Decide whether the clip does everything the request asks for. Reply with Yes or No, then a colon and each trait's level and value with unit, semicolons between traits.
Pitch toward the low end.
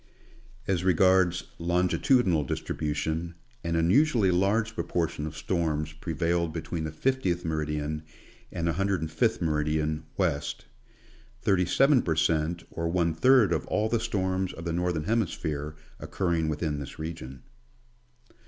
Yes: very low, 85 Hz